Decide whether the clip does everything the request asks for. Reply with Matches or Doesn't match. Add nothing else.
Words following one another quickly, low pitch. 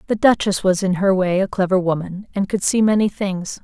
Doesn't match